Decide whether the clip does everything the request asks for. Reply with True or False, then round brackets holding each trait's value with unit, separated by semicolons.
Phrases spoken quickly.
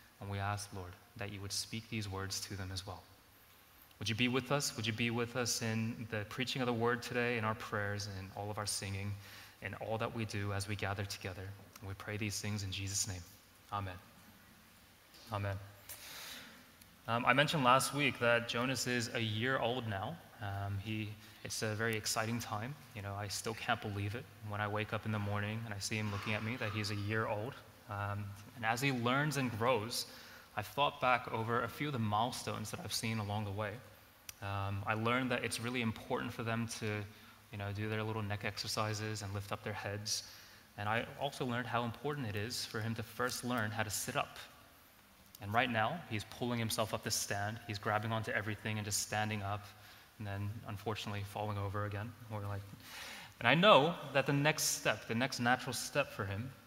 True (215 wpm)